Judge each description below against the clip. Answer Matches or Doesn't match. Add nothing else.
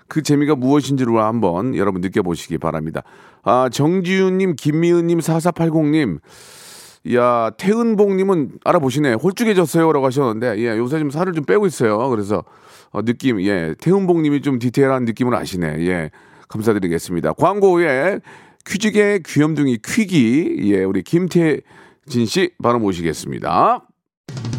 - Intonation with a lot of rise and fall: Matches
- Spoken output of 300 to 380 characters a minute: Matches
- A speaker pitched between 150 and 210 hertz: Doesn't match